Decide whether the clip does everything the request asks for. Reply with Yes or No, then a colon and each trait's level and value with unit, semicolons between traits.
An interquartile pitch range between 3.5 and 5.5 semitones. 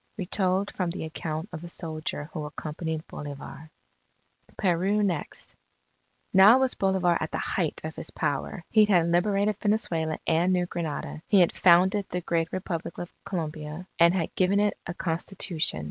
No: average, 3.1 semitones